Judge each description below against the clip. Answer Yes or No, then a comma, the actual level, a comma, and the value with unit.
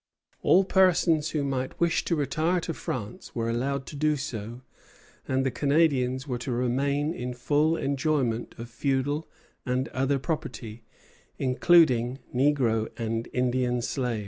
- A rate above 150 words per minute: No, average, 140 wpm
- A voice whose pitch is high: No, low, 135 Hz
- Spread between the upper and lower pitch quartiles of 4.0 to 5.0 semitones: No, average, 3.3 semitones